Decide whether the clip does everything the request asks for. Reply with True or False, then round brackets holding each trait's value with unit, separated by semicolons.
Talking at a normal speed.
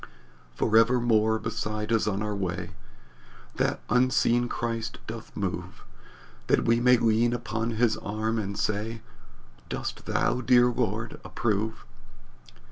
False (125 wpm)